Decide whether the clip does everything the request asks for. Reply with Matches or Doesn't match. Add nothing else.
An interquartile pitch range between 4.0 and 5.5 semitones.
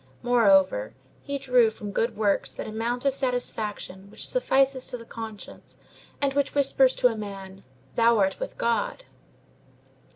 Matches